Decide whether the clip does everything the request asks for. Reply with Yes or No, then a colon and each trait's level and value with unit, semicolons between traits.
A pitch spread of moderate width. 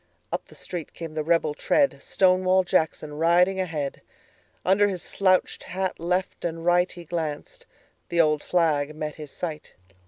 Yes: average, 3.0 semitones